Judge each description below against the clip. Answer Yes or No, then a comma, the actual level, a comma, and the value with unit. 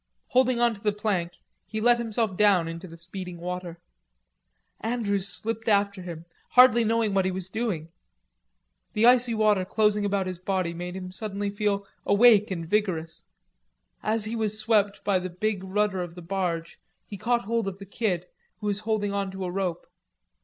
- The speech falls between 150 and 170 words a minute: No, average, 180 wpm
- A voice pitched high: Yes, high, 200 Hz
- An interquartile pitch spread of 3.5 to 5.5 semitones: No, average, 3.0 semitones